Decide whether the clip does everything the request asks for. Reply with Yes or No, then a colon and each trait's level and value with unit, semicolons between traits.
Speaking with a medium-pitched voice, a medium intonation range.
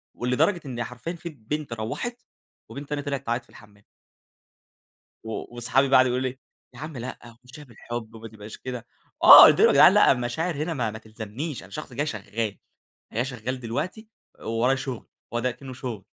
No: low, 125 Hz; average, 3.8 semitones